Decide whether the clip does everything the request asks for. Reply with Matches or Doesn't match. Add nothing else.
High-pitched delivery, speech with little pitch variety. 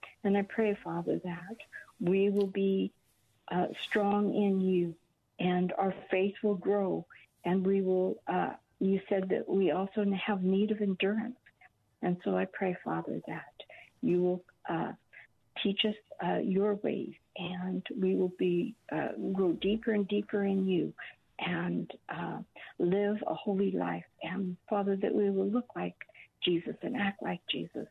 Matches